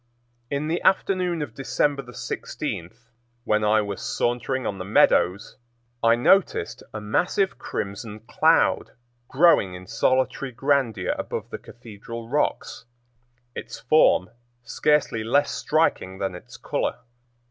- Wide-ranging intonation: Yes, wide, 5.7 semitones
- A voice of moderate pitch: No, low, 120 Hz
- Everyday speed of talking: No, slow, 120 wpm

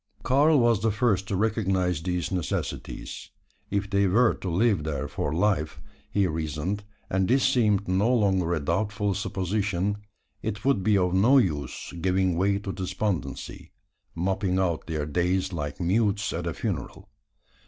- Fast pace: No, average, 155 wpm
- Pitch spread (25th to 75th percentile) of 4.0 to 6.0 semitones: No, average, 2.9 semitones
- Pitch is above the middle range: No, very low, 95 Hz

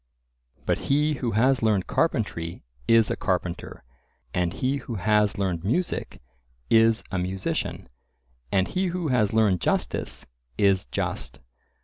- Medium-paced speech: No, slow, 130 wpm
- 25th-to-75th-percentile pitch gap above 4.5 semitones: Yes, average, 5.3 semitones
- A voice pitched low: Yes, low, 110 Hz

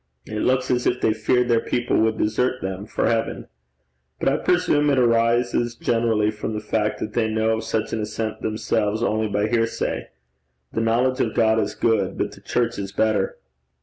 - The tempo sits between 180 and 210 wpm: Yes, average, 190 wpm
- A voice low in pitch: Yes, low, 115 Hz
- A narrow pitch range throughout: Yes, narrow, 1.9 semitones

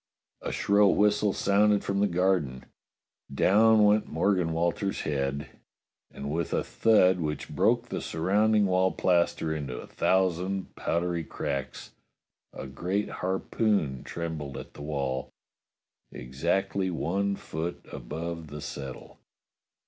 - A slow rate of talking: Yes, slow, 120 wpm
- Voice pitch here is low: Yes, very low, 90 Hz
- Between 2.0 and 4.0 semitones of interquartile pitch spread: No, average, 4.8 semitones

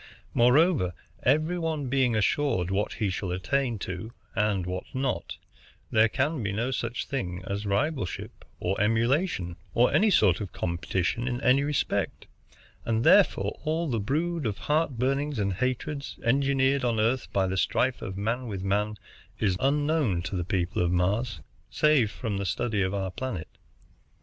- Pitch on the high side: No, low, 115 Hz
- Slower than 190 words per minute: Yes, average, 160 wpm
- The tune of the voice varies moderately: No, wide, 5.9 semitones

